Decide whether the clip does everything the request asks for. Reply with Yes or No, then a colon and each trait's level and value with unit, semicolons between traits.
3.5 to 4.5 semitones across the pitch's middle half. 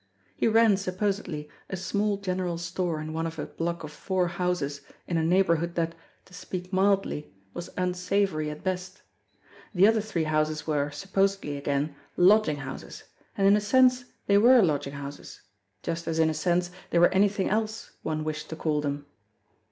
Yes: average, 4.1 semitones